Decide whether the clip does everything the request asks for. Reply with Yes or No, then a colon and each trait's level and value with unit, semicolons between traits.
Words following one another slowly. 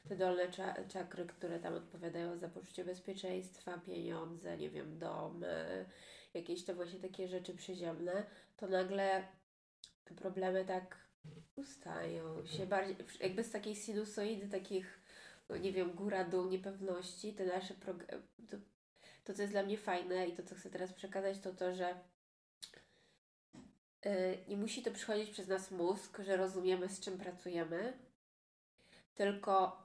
No: average, 140 wpm